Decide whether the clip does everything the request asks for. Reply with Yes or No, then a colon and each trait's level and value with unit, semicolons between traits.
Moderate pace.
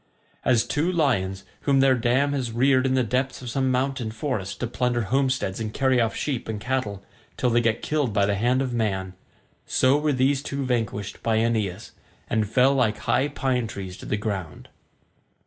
Yes: average, 190 wpm